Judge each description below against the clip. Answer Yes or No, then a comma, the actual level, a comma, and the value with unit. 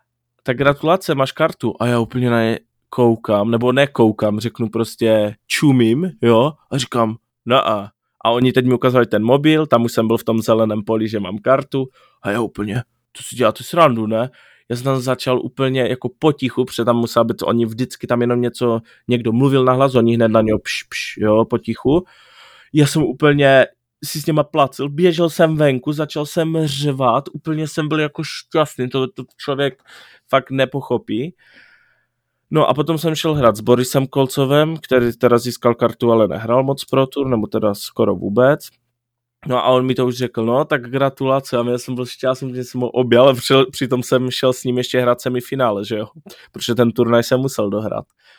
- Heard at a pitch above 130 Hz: No, low, 125 Hz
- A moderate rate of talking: No, fast, 190 wpm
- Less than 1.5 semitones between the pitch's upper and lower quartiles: No, average, 2.7 semitones